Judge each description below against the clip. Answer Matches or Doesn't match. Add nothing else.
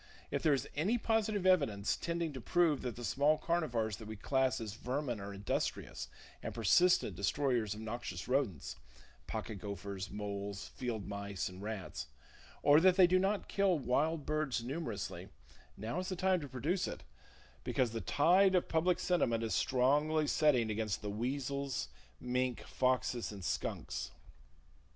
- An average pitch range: Doesn't match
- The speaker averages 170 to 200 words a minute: Doesn't match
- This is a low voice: Matches